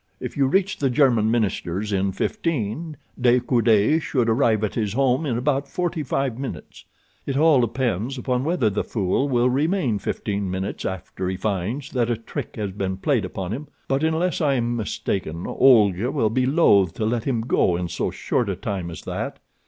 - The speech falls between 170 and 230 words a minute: Yes, average, 190 wpm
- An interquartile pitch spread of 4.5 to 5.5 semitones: Yes, average, 5.2 semitones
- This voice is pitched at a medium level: No, low, 120 Hz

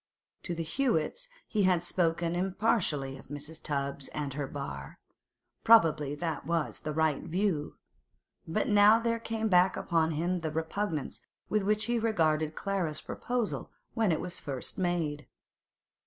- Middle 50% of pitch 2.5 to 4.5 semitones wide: No, average, 5.2 semitones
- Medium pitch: Yes, medium, 170 Hz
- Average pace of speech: Yes, average, 150 wpm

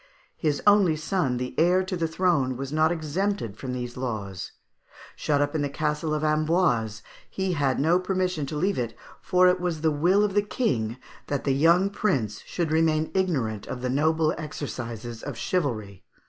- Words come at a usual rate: Yes, average, 180 wpm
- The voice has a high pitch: No, medium, 155 Hz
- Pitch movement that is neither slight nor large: No, wide, 5.9 semitones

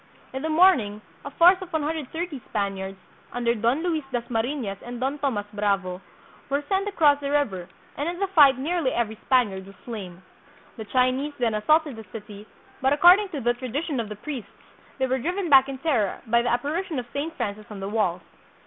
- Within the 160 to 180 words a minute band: No, average, 190 wpm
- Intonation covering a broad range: Yes, wide, 6.1 semitones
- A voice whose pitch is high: Yes, very high, 255 Hz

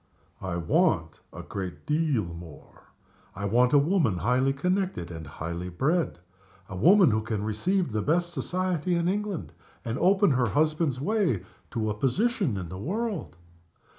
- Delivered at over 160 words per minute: No, average, 155 wpm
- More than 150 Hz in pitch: No, low, 135 Hz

